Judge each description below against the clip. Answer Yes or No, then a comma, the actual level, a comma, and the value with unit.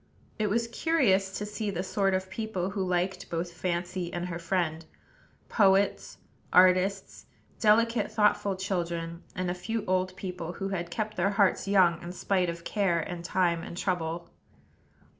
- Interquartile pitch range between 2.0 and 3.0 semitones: Yes, narrow, 2.5 semitones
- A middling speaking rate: Yes, average, 160 wpm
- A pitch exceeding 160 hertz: Yes, medium, 185 Hz